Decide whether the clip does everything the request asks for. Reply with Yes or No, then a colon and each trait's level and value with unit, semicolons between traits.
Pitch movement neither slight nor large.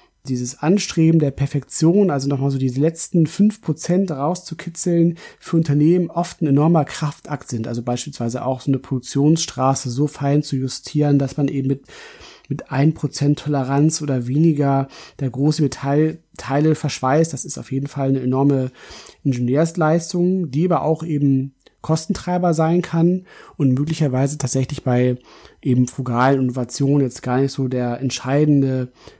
Yes: average, 3.2 semitones